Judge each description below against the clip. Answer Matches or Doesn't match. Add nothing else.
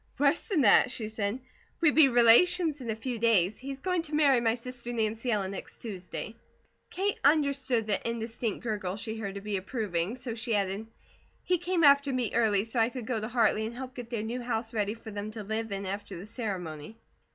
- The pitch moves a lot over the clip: Doesn't match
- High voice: Matches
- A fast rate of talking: Matches